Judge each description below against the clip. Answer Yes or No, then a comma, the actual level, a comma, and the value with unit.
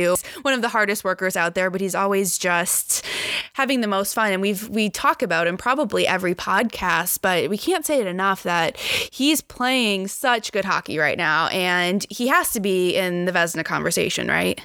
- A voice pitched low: No, high, 200 Hz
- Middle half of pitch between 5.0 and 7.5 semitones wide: Yes, wide, 5.6 semitones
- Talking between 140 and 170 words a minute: No, average, 195 wpm